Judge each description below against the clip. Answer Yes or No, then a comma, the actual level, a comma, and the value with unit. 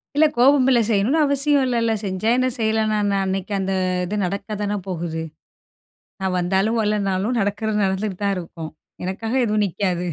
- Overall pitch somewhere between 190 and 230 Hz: Yes, high, 205 Hz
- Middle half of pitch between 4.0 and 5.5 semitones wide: No, average, 2.9 semitones